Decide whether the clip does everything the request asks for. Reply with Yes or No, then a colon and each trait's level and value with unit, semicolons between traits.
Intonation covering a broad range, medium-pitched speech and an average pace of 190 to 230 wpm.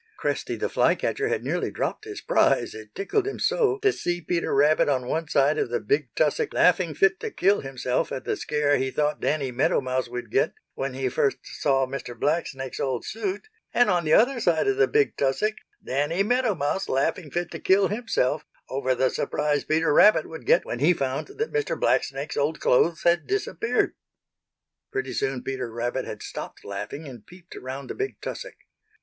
Yes: wide, 6.6 semitones; medium, 150 Hz; average, 195 wpm